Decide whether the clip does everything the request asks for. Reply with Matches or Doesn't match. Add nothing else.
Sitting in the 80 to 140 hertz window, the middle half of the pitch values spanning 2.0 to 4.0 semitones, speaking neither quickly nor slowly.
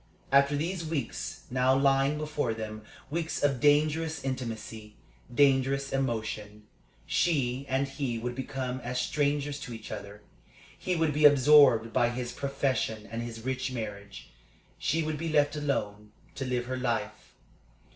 Matches